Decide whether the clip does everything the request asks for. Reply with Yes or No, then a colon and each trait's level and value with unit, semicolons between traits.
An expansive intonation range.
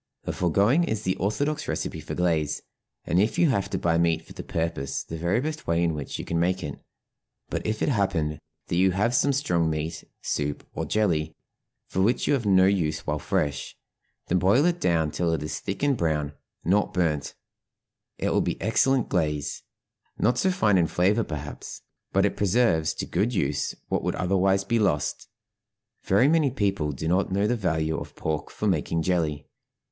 No: average, 5.0 semitones